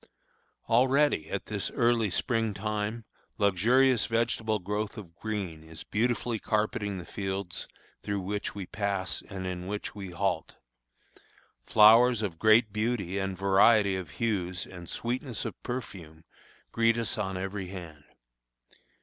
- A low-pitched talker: Yes, low, 105 Hz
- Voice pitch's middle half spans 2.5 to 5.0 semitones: Yes, average, 3.4 semitones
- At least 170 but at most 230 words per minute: No, slow, 135 wpm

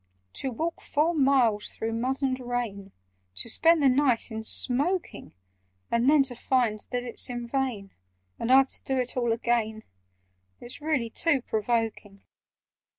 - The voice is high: Yes, high, 245 Hz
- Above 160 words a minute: No, average, 150 wpm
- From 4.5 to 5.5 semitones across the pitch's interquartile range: No, average, 3.1 semitones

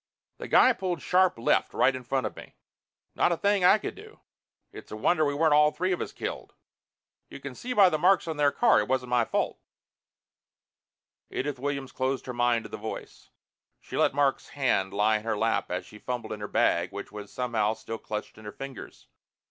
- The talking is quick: Yes, fast, 215 wpm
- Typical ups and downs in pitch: No, wide, 5.7 semitones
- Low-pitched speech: Yes, low, 130 Hz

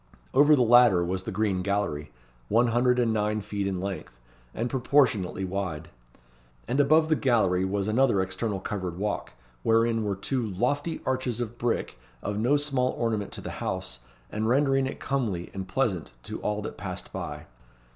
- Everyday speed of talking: Yes, average, 170 wpm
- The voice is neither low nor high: No, low, 110 Hz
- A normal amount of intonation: Yes, average, 4.5 semitones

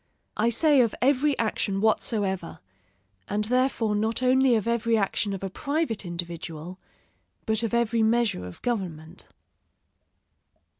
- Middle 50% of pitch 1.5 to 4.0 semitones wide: Yes, average, 3.7 semitones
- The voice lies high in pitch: Yes, high, 220 Hz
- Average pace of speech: No, slow, 130 wpm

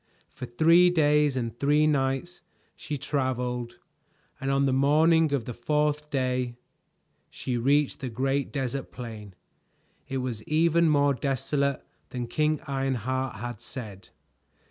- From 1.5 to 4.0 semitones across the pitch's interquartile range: Yes, average, 3.2 semitones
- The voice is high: No, low, 135 Hz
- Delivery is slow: Yes, slow, 130 wpm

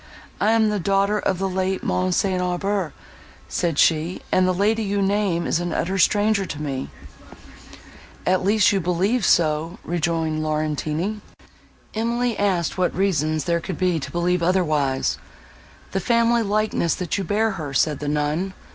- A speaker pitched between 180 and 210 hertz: Yes, medium, 185 Hz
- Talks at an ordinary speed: Yes, average, 160 wpm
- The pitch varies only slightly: No, average, 3.8 semitones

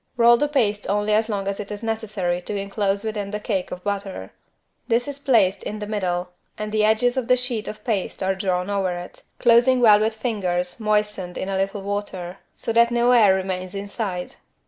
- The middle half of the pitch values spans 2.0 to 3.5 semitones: Yes, average, 2.7 semitones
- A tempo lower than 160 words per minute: No, fast, 205 wpm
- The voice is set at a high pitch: Yes, high, 205 Hz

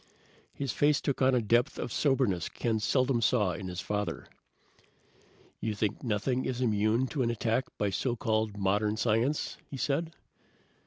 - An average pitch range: Yes, average, 3.7 semitones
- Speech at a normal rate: Yes, average, 160 wpm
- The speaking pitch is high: No, low, 115 Hz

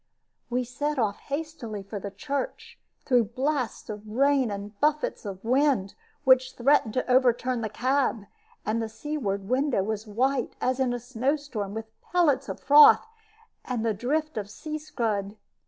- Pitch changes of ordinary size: Yes, average, 4.6 semitones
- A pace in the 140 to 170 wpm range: Yes, average, 155 wpm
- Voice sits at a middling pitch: No, very high, 250 Hz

